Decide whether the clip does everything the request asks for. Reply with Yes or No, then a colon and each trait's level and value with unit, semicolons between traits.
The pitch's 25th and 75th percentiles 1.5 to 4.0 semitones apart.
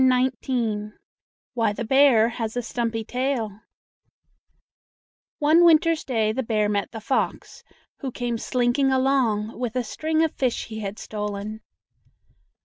Yes: average, 3.6 semitones